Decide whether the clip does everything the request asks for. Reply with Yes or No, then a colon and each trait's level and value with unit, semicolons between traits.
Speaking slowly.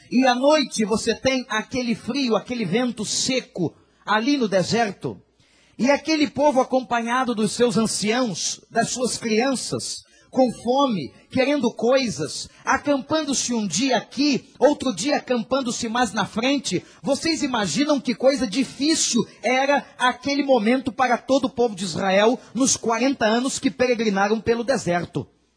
No: average, 135 wpm